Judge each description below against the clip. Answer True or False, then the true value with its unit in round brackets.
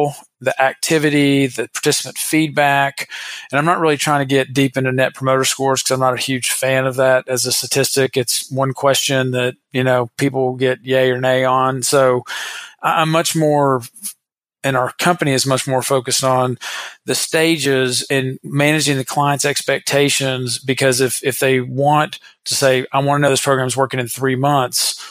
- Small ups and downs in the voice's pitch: True (1.7 semitones)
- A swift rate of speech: False (185 wpm)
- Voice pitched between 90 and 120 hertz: False (135 Hz)